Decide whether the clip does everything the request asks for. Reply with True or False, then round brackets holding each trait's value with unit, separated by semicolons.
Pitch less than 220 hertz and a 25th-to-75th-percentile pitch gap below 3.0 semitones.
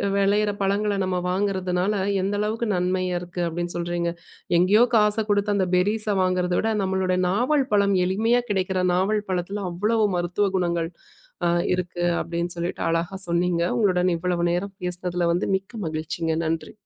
True (185 Hz; 2.6 semitones)